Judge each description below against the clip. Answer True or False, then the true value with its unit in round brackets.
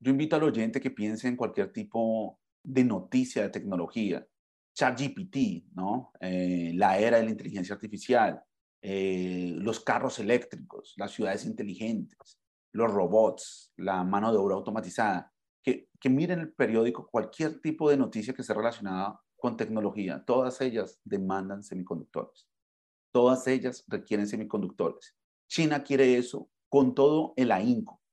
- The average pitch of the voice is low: True (115 Hz)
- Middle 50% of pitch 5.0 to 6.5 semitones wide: True (5.6 semitones)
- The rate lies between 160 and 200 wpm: False (140 wpm)